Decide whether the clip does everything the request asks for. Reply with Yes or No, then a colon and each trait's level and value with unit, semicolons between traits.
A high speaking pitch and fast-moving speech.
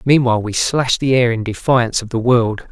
No: low, 120 Hz; fast, 220 wpm